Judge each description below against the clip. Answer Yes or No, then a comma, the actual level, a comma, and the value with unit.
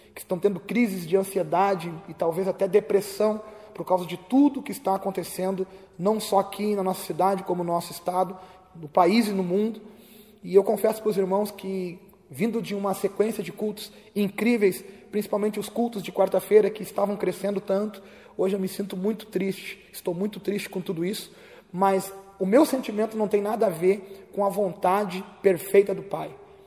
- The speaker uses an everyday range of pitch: No, narrow, 1.9 semitones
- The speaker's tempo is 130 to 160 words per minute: No, fast, 185 wpm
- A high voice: Yes, high, 195 Hz